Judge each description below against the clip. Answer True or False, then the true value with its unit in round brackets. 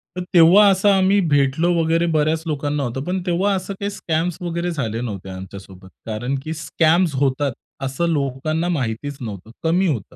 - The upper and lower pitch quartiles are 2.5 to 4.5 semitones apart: False (5.0 semitones)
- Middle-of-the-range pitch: True (155 Hz)